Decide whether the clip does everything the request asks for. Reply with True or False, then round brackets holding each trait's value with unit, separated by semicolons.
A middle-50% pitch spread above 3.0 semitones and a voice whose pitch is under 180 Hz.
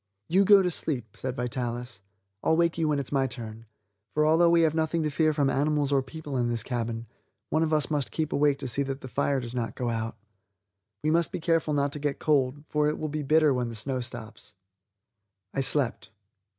True (4.0 semitones; 140 Hz)